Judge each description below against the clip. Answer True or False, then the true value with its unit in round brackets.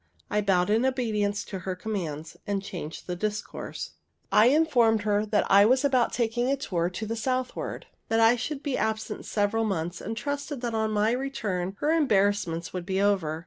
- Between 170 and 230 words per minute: True (185 wpm)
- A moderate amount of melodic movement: True (4.0 semitones)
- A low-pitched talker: False (215 Hz)